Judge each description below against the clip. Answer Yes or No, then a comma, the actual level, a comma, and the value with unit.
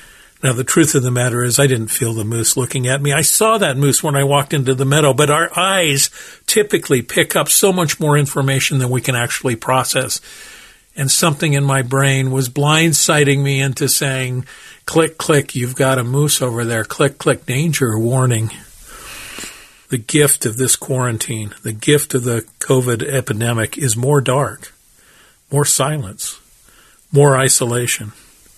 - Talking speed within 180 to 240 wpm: No, average, 170 wpm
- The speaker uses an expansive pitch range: No, average, 2.7 semitones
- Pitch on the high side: No, low, 135 Hz